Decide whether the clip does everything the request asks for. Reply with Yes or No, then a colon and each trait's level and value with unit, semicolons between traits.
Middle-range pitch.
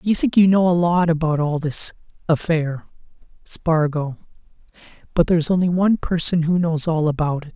Yes: medium, 165 Hz